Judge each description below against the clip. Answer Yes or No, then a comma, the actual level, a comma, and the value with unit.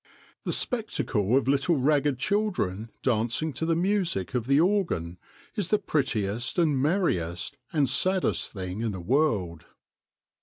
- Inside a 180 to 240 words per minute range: No, average, 140 wpm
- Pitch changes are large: Yes, wide, 8.4 semitones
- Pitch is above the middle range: No, low, 135 Hz